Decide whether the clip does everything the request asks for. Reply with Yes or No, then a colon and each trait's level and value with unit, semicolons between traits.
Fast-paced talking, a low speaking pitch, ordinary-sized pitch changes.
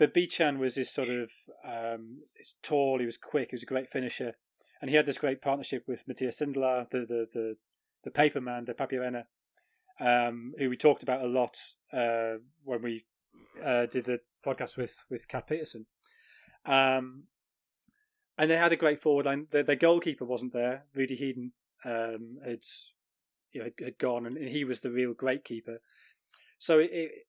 No: average, 180 wpm; low, 130 Hz; average, 3.1 semitones